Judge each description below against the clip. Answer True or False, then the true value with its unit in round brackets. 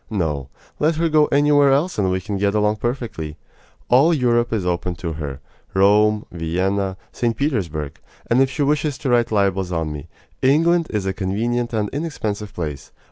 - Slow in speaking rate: False (175 wpm)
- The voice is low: True (105 Hz)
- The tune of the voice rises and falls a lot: True (6.7 semitones)